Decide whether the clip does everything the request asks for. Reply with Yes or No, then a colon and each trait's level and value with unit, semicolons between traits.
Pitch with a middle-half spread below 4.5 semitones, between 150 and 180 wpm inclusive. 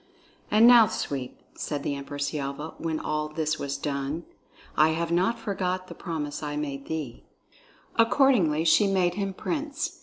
No: average, 5.0 semitones; average, 160 wpm